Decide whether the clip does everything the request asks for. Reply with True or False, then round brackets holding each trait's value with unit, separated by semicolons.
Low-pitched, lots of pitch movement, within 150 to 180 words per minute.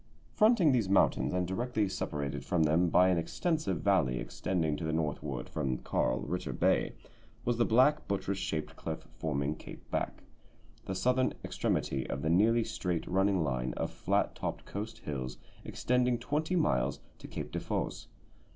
True (90 Hz; 7.6 semitones; 160 wpm)